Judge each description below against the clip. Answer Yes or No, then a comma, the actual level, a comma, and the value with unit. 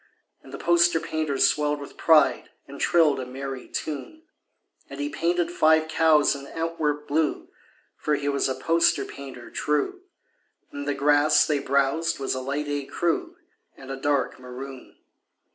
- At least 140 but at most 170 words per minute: Yes, average, 155 wpm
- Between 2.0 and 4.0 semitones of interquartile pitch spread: Yes, average, 2.7 semitones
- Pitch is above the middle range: No, medium, 145 Hz